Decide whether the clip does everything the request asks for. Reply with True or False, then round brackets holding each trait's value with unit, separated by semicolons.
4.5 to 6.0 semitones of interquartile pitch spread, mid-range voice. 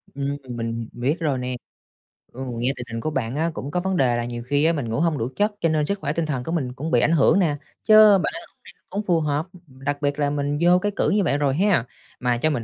True (4.9 semitones; 145 Hz)